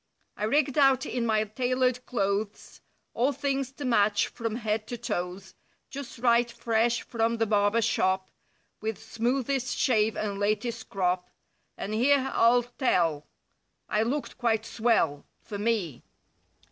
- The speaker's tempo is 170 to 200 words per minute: No, slow, 135 wpm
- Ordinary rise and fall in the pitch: Yes, average, 3.0 semitones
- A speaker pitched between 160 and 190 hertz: No, high, 230 Hz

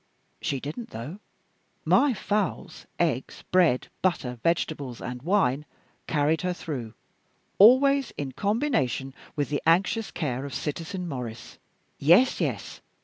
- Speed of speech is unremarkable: No, slow, 120 wpm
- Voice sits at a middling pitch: Yes, medium, 160 Hz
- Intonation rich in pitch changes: Yes, wide, 6.7 semitones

